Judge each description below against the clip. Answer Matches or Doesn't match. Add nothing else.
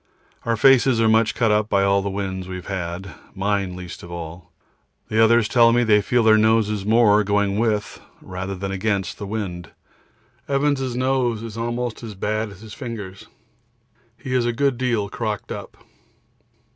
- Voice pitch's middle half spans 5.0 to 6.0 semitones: Doesn't match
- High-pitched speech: Doesn't match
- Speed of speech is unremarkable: Matches